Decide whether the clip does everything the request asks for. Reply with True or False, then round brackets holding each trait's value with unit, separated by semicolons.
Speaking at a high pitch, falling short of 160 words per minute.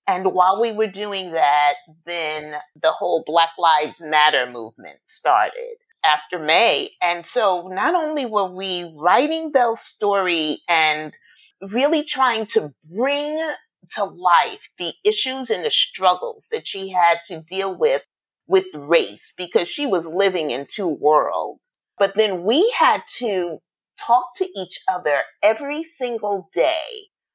True (195 Hz; 140 wpm)